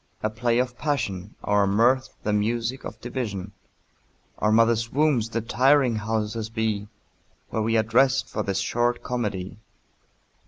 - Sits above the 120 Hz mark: No, low, 115 Hz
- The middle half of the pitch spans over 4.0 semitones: No, narrow, 2.5 semitones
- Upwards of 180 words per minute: No, average, 145 wpm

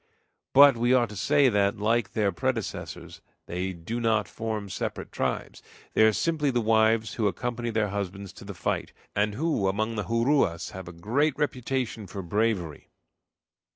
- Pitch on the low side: Yes, low, 110 Hz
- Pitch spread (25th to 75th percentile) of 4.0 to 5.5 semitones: No, average, 3.3 semitones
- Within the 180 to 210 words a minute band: No, average, 165 wpm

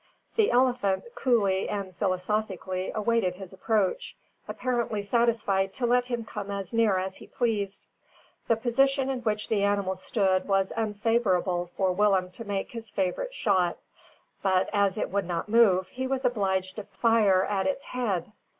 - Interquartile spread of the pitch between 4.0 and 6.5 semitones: No, average, 3.4 semitones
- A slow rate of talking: No, average, 160 wpm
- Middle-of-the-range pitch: No, high, 205 Hz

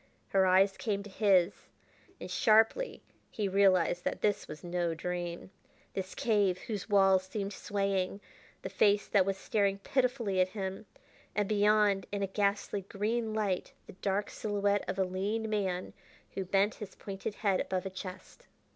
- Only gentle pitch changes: Yes, narrow, 1.7 semitones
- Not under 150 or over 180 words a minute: Yes, average, 160 wpm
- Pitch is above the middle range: Yes, high, 195 Hz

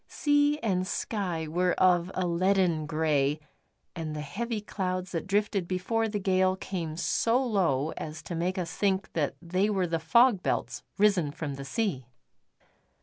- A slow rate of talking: No, average, 160 wpm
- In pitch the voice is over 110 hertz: Yes, medium, 185 Hz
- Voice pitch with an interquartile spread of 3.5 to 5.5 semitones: Yes, average, 3.9 semitones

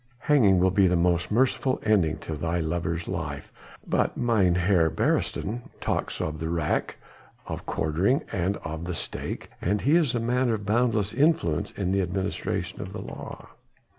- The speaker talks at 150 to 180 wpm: Yes, average, 165 wpm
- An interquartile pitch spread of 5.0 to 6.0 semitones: Yes, average, 5.3 semitones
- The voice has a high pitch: No, very low, 95 Hz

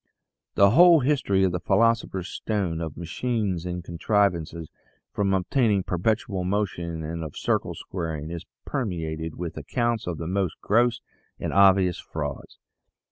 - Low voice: Yes, very low, 95 Hz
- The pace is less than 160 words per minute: Yes, slow, 135 wpm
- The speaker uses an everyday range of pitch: Yes, average, 4.2 semitones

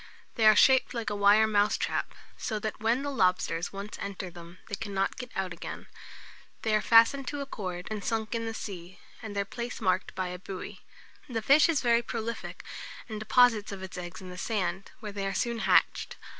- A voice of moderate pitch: No, high, 210 Hz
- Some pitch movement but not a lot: Yes, average, 3.4 semitones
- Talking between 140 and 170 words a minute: No, fast, 205 wpm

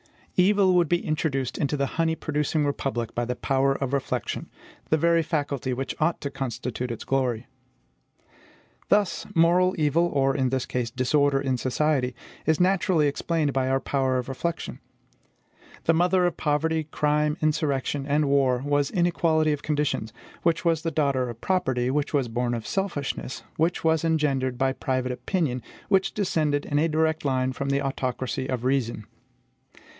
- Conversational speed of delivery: Yes, average, 160 wpm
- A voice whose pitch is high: No, medium, 145 Hz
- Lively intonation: No, average, 3.6 semitones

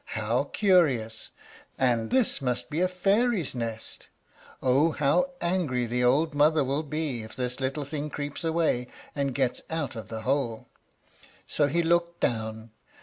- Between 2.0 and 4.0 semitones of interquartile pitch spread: No, average, 4.8 semitones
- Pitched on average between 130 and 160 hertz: Yes, medium, 140 Hz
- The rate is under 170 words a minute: Yes, average, 150 wpm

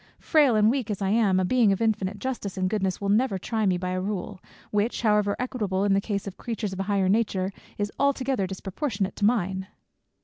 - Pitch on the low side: No, high, 205 Hz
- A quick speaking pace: Yes, fast, 215 wpm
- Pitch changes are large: No, average, 2.9 semitones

